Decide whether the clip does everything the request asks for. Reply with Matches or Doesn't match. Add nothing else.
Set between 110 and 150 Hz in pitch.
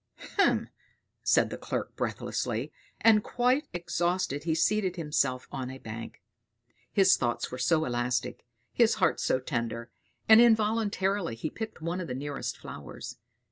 Doesn't match